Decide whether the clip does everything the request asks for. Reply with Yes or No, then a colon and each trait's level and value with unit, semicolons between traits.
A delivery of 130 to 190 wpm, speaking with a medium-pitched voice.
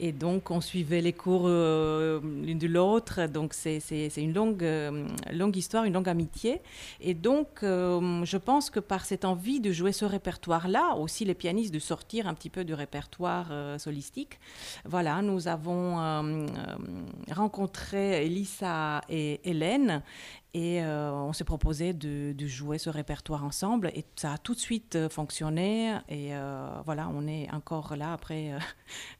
Yes: average, 170 wpm; medium, 170 Hz